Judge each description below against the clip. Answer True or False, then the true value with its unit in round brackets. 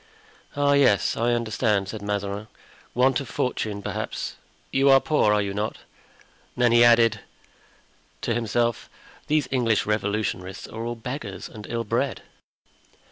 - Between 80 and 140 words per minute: True (135 wpm)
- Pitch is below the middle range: True (115 Hz)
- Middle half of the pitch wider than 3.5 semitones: False (2.9 semitones)